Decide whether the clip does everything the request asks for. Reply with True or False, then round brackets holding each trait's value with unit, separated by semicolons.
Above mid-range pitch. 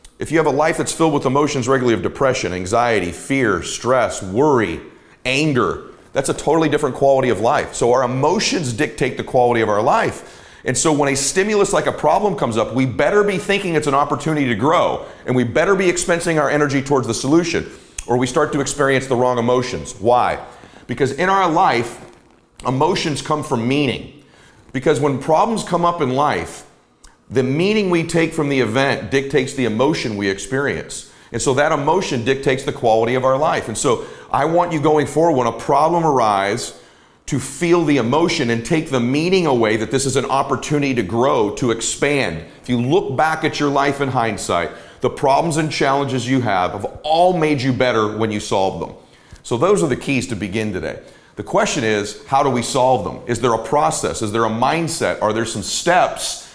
False (140 Hz)